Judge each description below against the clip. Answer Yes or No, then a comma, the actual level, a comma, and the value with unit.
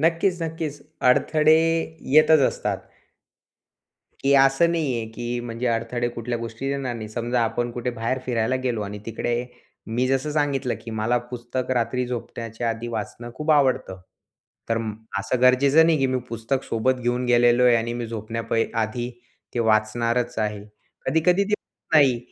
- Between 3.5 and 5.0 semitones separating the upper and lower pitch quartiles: No, average, 2.7 semitones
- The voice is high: No, low, 120 Hz